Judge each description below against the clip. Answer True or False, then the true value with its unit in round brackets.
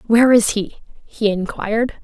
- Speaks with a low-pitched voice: False (220 Hz)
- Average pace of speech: True (145 wpm)